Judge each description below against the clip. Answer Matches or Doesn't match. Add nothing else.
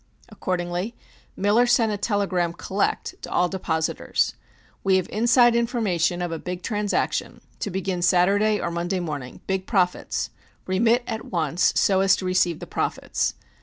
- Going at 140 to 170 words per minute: Matches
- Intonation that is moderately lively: Matches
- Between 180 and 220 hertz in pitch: Matches